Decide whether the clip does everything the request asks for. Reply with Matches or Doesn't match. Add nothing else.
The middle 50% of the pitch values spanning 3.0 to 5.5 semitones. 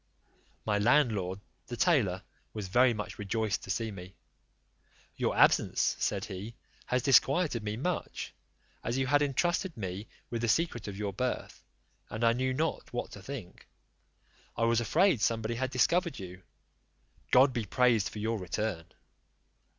Matches